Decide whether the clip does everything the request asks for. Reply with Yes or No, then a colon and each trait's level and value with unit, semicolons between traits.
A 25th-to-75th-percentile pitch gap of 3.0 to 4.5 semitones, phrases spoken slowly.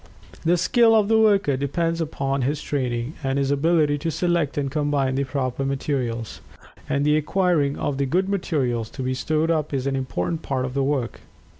No: average, 3.6 semitones; average, 185 wpm